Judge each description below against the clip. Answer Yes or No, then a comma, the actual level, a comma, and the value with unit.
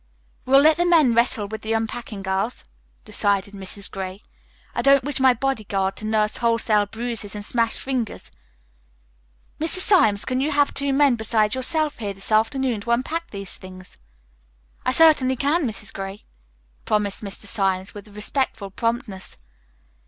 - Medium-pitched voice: No, high, 225 Hz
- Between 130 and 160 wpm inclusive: Yes, average, 155 wpm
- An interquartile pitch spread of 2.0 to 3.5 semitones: No, average, 4.7 semitones